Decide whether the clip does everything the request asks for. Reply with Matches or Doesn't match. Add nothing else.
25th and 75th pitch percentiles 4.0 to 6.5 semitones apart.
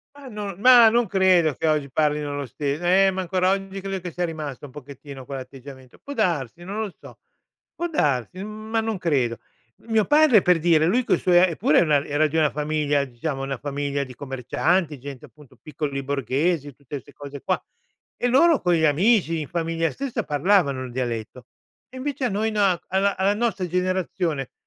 Matches